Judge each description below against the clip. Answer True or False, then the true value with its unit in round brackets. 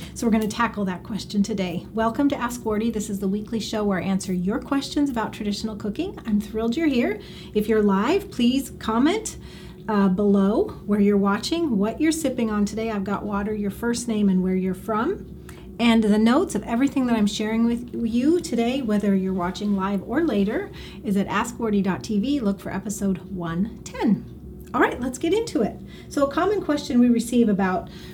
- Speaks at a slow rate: False (195 wpm)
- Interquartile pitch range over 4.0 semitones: False (3.3 semitones)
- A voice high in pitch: True (215 Hz)